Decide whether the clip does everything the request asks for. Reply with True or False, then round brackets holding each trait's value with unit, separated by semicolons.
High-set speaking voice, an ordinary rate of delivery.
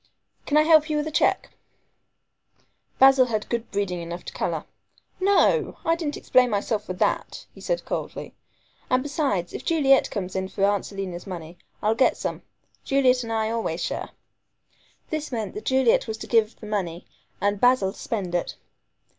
True (225 Hz; 175 wpm)